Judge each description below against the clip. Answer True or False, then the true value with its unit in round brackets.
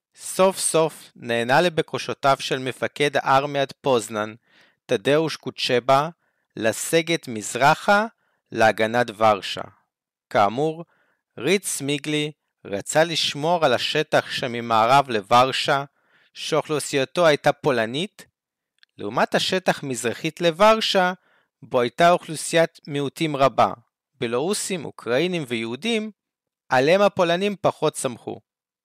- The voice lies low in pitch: False (145 Hz)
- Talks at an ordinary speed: False (85 wpm)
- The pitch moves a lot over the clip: True (5.9 semitones)